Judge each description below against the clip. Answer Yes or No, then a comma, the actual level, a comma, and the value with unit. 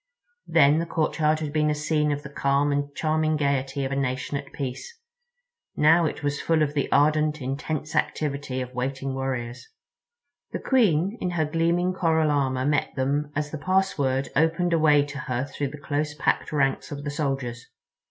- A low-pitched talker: No, medium, 145 Hz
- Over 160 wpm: Yes, average, 180 wpm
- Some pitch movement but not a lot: No, narrow, 2.3 semitones